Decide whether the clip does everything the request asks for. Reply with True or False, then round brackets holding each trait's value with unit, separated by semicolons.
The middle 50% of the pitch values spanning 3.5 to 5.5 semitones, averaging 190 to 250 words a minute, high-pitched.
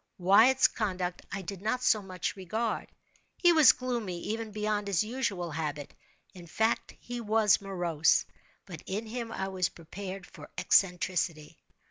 False (3.9 semitones; 135 wpm; 200 Hz)